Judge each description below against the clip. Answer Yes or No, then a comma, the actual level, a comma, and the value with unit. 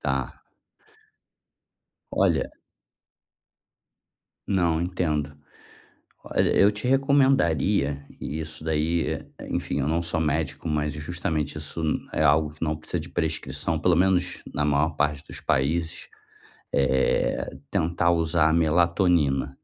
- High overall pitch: No, very low, 80 Hz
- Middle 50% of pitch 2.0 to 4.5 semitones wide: Yes, narrow, 2.5 semitones